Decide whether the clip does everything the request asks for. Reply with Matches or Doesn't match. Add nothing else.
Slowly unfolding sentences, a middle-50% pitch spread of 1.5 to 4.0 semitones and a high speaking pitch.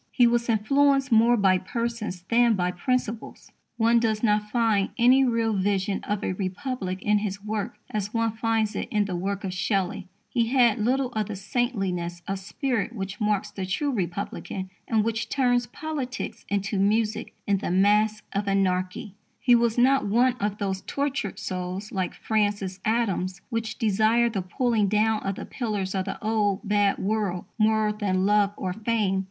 Doesn't match